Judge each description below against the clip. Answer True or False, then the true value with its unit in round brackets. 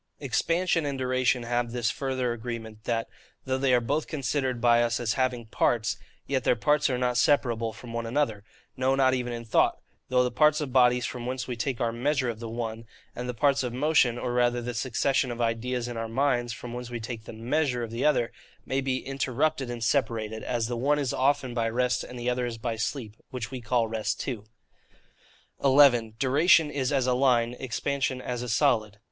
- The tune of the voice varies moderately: False (2.3 semitones)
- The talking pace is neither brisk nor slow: False (210 wpm)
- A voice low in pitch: True (125 Hz)